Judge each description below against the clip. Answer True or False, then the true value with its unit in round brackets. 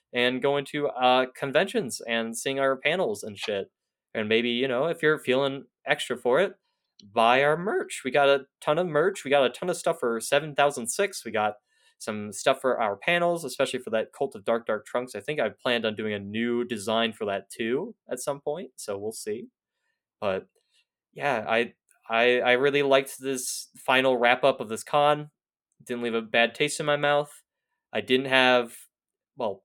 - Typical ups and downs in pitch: True (3.6 semitones)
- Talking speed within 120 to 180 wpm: False (200 wpm)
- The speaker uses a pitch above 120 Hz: True (135 Hz)